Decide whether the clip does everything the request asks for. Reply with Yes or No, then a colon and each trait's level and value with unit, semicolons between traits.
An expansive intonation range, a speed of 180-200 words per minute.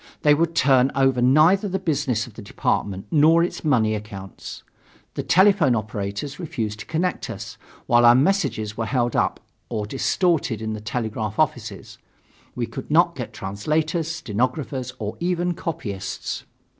No: wide, 6.8 semitones; average, 155 wpm